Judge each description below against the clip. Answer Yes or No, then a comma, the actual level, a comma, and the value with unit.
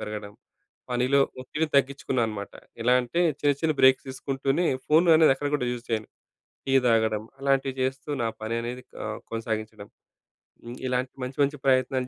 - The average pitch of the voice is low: Yes, low, 130 Hz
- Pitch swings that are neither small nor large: Yes, average, 3.0 semitones